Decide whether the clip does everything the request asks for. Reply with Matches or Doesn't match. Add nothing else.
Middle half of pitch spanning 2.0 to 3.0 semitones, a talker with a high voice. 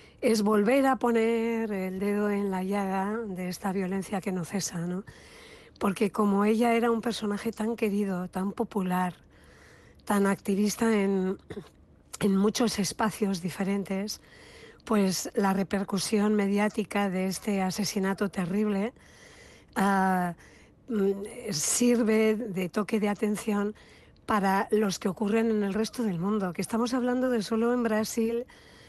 Matches